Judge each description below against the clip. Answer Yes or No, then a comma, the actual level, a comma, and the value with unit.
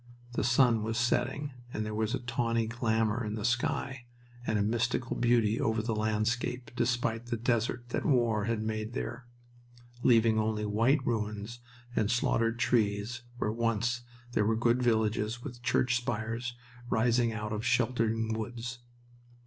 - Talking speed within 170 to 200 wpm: No, average, 150 wpm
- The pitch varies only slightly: Yes, narrow, 1.8 semitones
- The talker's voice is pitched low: Yes, low, 115 Hz